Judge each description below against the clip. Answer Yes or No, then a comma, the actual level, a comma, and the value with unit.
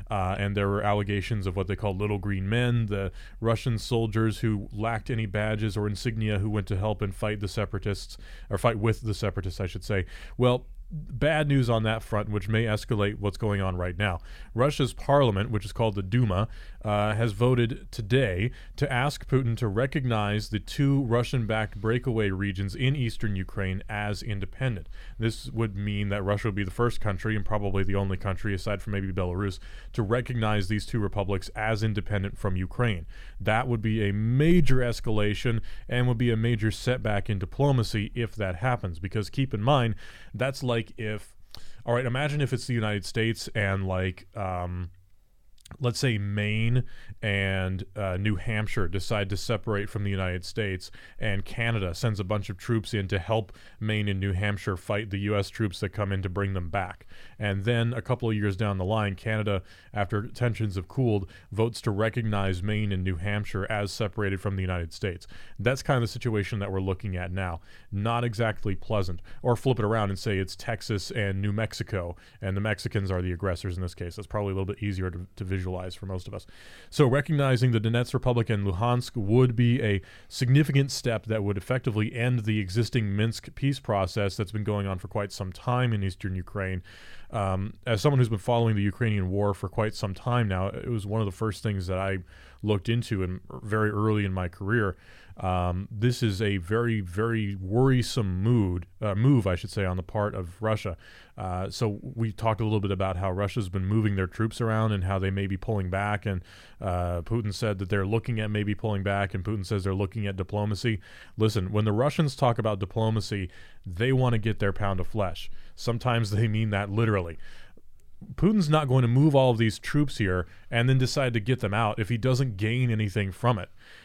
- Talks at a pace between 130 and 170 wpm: No, fast, 205 wpm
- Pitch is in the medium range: No, low, 105 Hz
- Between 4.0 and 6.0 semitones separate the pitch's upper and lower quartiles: No, average, 2.9 semitones